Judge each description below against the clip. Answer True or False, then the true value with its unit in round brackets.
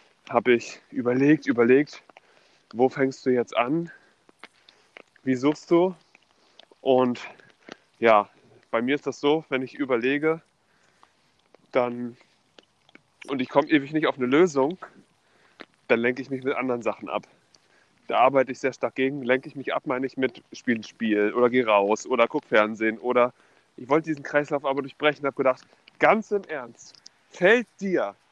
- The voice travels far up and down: False (3.1 semitones)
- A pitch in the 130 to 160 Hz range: True (135 Hz)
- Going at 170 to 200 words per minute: False (155 wpm)